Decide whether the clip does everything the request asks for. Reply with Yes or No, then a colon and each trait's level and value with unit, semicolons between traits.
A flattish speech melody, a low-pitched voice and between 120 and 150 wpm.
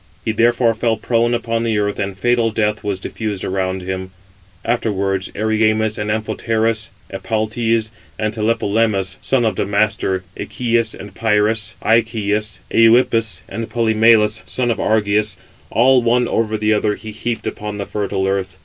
Yes: narrow, 1.9 semitones; low, 110 Hz; average, 145 wpm